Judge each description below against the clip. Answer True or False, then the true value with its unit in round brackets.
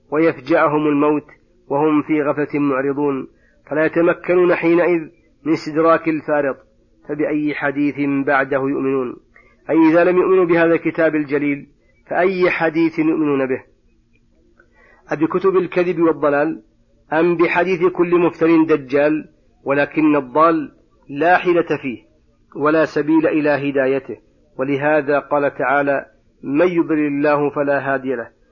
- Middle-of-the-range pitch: True (150 Hz)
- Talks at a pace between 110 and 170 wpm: True (115 wpm)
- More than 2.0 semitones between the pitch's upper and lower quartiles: True (2.5 semitones)